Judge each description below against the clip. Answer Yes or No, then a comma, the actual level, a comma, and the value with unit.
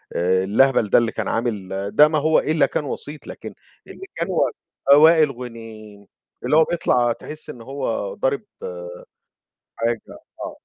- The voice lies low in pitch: Yes, low, 125 Hz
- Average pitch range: No, wide, 6.0 semitones